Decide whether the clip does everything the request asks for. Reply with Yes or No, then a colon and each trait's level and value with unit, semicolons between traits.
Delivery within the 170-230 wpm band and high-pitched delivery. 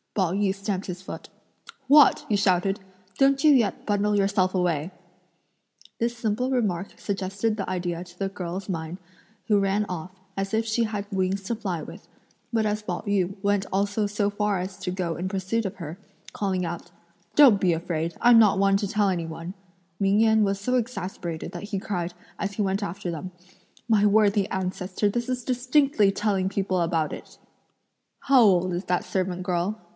Yes: average, 180 wpm; high, 195 Hz